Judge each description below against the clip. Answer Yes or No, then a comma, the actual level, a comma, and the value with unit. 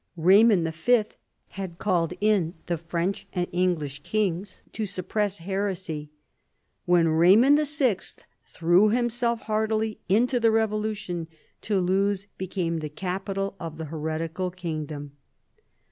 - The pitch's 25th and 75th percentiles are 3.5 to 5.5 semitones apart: Yes, average, 4.2 semitones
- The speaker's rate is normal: No, slow, 115 wpm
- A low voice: No, medium, 185 Hz